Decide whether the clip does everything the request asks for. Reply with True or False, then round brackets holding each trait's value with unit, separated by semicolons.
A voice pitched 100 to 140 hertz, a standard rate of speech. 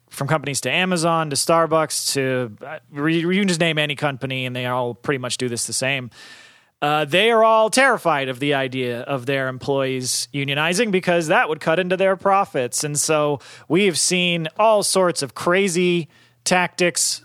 False (150 Hz; 175 wpm)